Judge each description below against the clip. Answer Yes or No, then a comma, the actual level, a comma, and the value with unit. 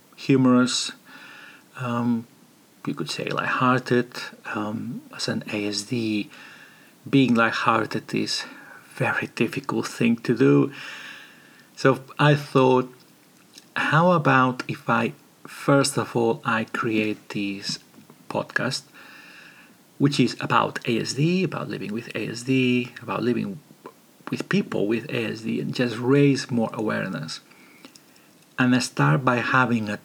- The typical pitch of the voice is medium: No, low, 125 Hz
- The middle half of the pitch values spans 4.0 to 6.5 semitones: No, average, 2.7 semitones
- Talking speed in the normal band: No, slow, 120 wpm